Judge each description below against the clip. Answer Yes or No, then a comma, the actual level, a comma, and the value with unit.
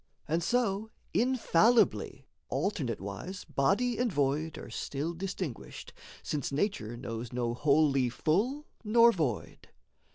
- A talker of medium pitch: Yes, medium, 160 Hz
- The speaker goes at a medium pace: No, slow, 110 wpm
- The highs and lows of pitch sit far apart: Yes, wide, 7.9 semitones